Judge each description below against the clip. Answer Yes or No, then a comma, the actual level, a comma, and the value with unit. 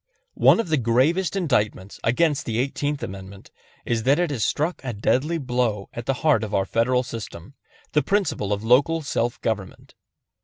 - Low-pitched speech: Yes, low, 125 Hz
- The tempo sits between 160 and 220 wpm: Yes, average, 170 wpm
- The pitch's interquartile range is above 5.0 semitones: Yes, wide, 5.4 semitones